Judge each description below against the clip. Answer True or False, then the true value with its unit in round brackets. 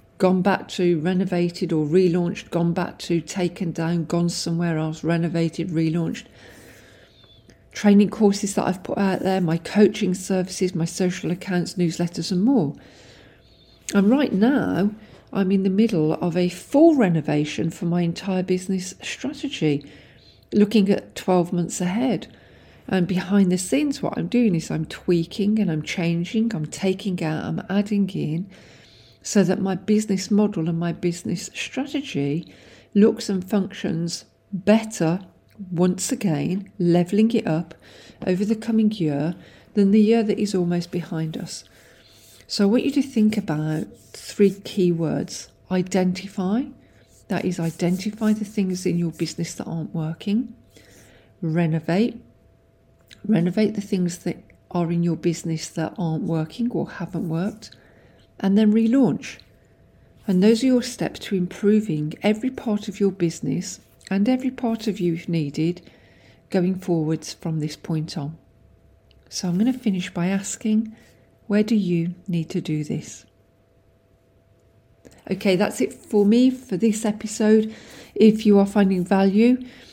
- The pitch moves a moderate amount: True (3.8 semitones)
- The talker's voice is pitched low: False (185 Hz)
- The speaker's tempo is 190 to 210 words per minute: False (145 wpm)